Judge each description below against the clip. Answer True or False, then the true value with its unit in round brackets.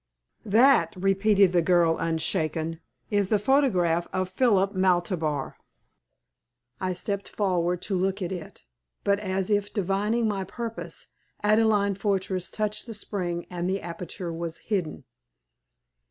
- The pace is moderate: False (125 wpm)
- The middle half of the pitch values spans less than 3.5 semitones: True (2.9 semitones)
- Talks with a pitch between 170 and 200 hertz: True (190 Hz)